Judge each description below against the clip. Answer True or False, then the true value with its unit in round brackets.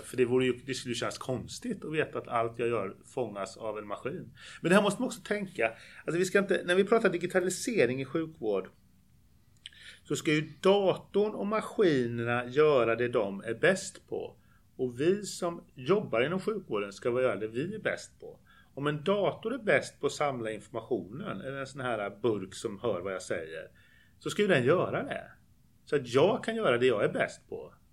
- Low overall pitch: False (155 Hz)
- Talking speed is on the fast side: True (205 wpm)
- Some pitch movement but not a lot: False (8.2 semitones)